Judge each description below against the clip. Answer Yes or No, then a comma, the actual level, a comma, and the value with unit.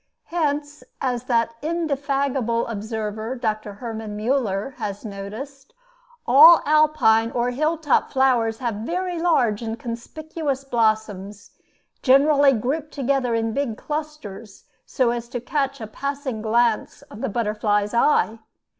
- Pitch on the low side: No, high, 245 Hz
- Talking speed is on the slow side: Yes, slow, 125 wpm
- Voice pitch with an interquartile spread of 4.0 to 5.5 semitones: Yes, average, 4.3 semitones